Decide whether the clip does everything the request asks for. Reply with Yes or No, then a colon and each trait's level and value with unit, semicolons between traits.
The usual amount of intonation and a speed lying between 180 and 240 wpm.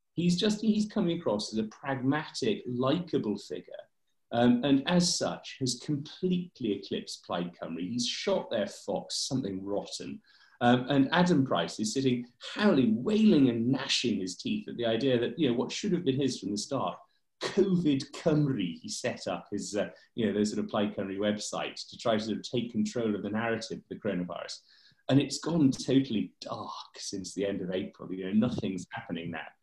No: wide, 6.9 semitones; average, 190 wpm